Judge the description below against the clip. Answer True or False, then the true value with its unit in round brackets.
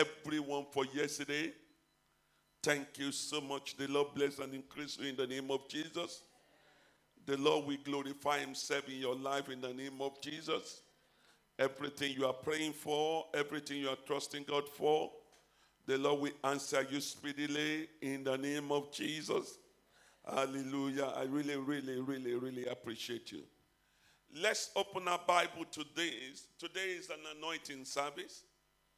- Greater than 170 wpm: False (145 wpm)